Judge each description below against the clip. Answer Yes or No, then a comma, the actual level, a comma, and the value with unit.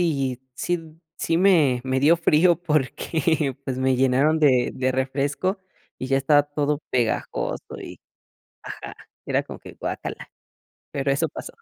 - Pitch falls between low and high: Yes, medium, 145 Hz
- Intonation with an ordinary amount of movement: Yes, average, 3.4 semitones